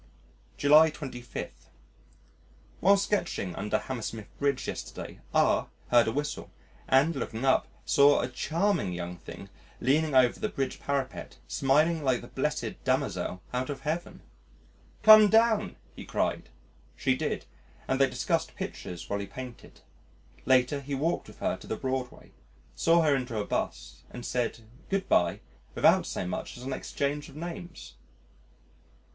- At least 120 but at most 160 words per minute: Yes, average, 145 wpm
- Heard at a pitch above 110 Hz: Yes, low, 135 Hz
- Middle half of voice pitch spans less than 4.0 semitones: No, average, 4.4 semitones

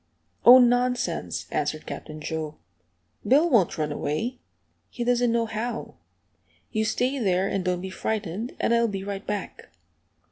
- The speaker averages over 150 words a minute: No, average, 145 wpm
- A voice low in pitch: No, high, 220 Hz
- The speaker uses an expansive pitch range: No, average, 4.7 semitones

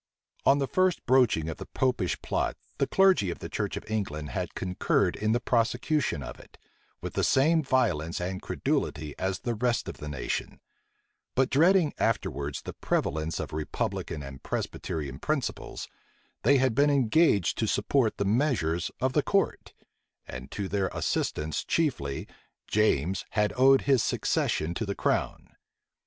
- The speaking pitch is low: Yes, low, 110 Hz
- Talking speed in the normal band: Yes, average, 155 wpm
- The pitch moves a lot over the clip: Yes, wide, 8.9 semitones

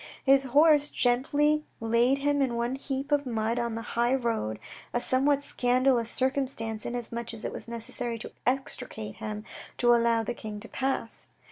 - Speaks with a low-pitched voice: No, high, 245 Hz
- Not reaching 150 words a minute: No, average, 170 wpm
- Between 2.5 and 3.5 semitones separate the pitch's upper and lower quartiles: Yes, average, 2.8 semitones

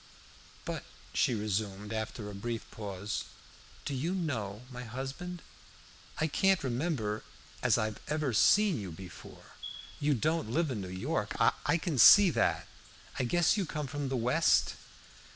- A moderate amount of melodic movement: No, wide, 6.7 semitones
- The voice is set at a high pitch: No, low, 130 Hz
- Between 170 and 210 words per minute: No, average, 150 wpm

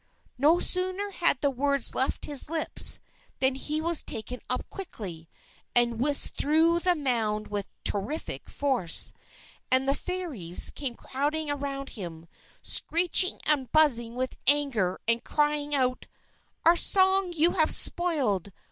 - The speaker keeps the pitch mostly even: No, average, 5.3 semitones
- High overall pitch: Yes, very high, 280 Hz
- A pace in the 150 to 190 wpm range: No, average, 140 wpm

